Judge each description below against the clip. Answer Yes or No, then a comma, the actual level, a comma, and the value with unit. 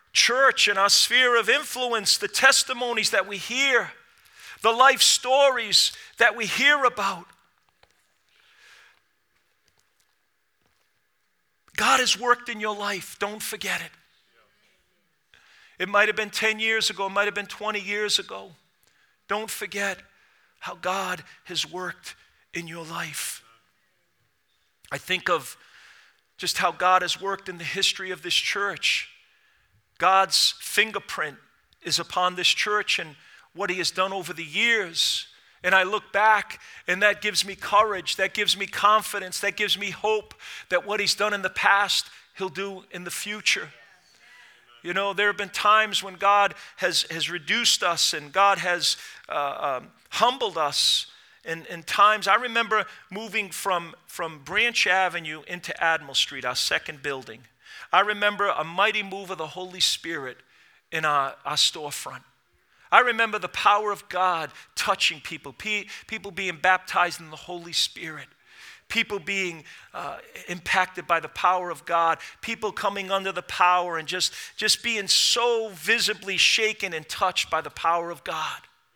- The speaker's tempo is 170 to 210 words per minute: No, average, 150 wpm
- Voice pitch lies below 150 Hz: No, high, 200 Hz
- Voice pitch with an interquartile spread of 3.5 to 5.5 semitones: No, average, 3.1 semitones